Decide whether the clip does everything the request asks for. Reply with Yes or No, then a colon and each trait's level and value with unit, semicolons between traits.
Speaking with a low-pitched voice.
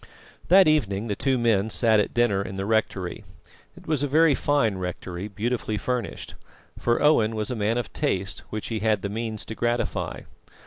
Yes: low, 110 Hz